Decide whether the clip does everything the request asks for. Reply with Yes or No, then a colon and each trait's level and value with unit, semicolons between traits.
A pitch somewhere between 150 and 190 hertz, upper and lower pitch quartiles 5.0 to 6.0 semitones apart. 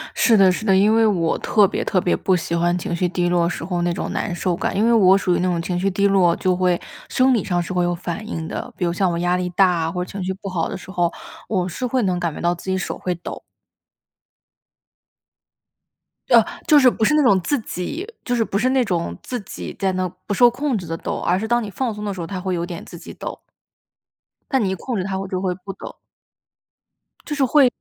No: medium, 185 Hz; average, 3.6 semitones